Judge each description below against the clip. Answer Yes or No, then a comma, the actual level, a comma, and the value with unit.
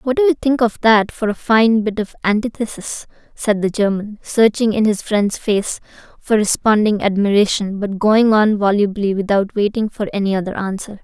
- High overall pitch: Yes, high, 210 Hz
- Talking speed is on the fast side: No, average, 180 wpm